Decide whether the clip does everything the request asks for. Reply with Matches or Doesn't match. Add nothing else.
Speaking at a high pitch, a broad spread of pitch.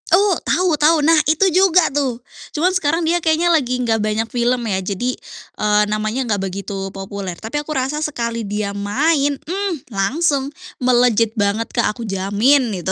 Matches